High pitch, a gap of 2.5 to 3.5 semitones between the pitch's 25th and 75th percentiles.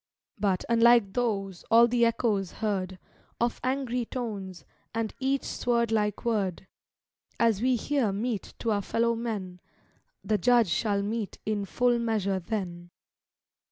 Yes: high, 220 Hz; average, 3.2 semitones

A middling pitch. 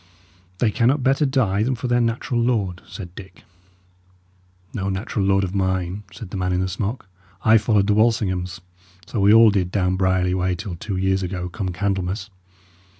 No: very low, 95 Hz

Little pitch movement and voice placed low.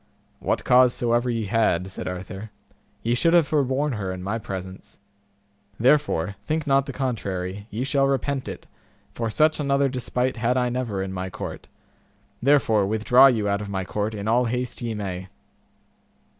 No: average, 4.8 semitones; low, 115 Hz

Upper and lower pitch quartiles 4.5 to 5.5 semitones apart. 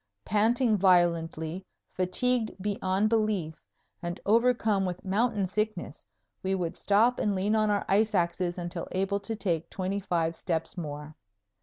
No: average, 3.6 semitones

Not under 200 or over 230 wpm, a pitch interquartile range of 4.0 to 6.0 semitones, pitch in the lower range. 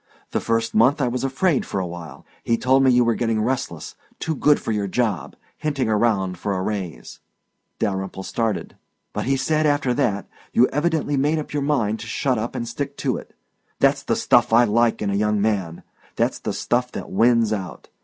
Yes: fast, 205 wpm; average, 4.6 semitones; low, 115 Hz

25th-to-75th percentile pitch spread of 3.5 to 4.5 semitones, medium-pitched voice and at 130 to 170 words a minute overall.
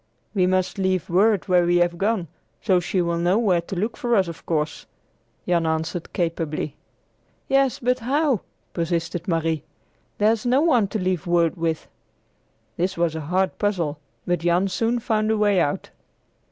Yes: average, 4.1 semitones; medium, 180 Hz; average, 165 wpm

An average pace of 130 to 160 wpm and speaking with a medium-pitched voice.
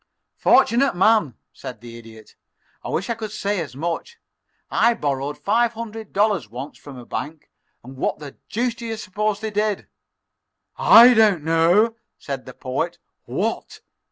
No: average, 155 wpm; high, 200 Hz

